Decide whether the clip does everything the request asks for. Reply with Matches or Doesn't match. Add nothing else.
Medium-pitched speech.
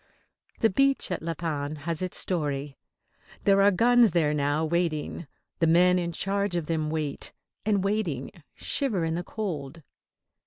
Matches